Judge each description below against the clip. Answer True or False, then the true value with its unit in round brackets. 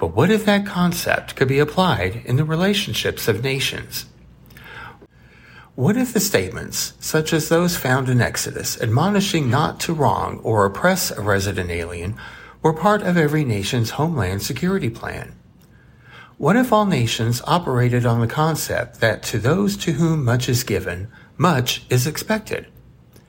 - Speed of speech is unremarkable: True (150 wpm)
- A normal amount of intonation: False (6.9 semitones)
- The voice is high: False (135 Hz)